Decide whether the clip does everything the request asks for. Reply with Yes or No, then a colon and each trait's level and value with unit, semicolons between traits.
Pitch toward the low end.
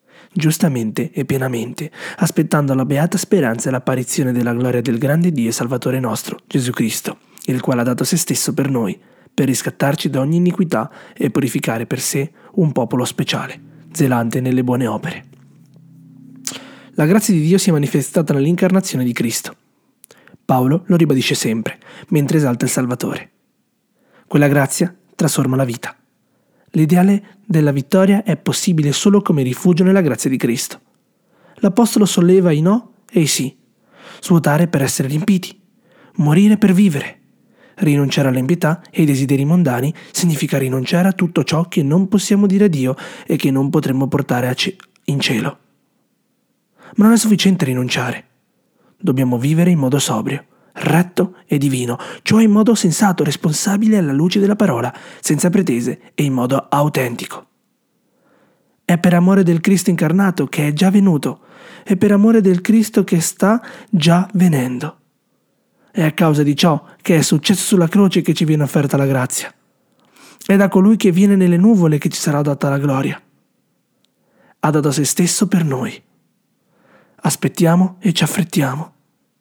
No: medium, 170 Hz